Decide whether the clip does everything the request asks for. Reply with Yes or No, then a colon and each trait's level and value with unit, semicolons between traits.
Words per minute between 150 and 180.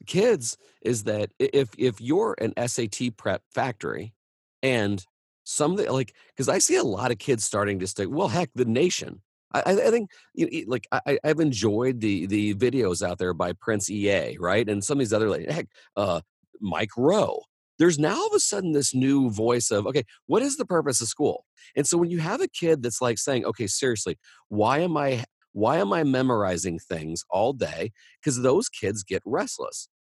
No: average, 200 wpm